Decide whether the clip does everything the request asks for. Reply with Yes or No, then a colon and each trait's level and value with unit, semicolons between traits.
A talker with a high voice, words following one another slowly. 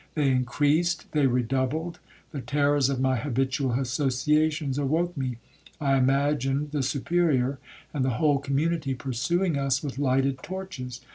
No: medium, 140 Hz; slow, 130 wpm